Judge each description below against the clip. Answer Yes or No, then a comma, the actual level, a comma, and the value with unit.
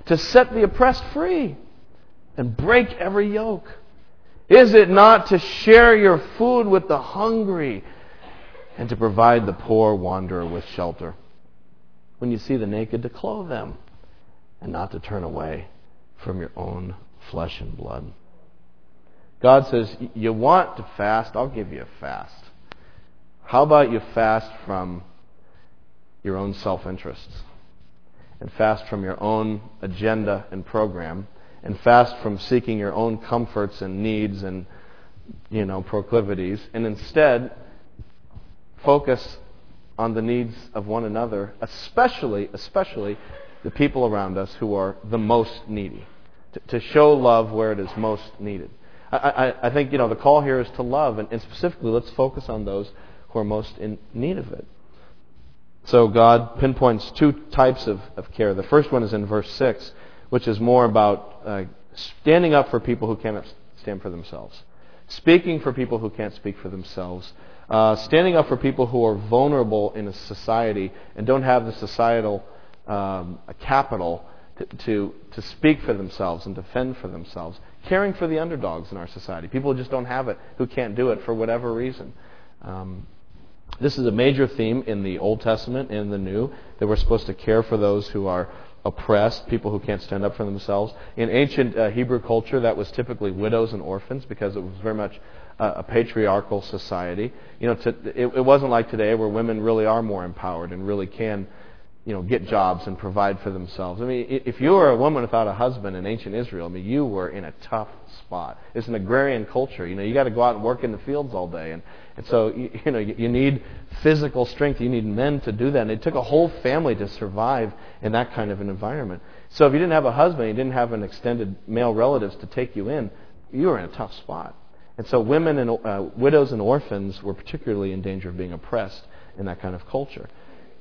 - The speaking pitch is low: Yes, low, 110 Hz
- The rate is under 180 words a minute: No, average, 190 wpm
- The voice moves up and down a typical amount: Yes, average, 4.4 semitones